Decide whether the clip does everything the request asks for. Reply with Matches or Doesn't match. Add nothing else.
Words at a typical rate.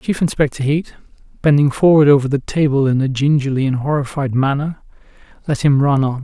Matches